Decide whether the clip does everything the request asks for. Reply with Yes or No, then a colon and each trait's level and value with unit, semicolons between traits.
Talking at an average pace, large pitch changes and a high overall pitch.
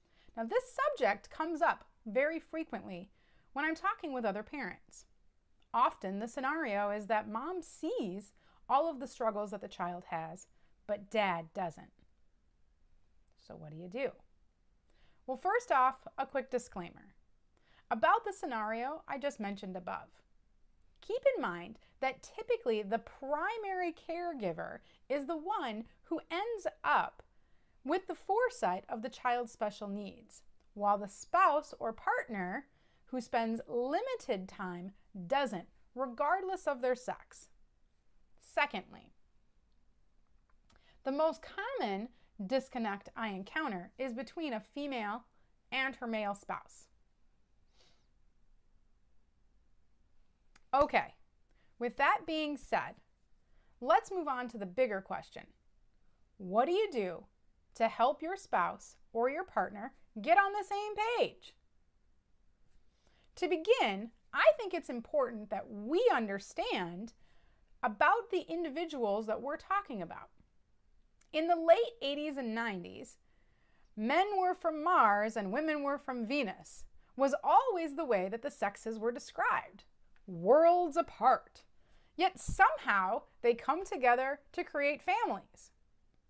No: slow, 125 wpm; wide, 7.6 semitones; very high, 265 Hz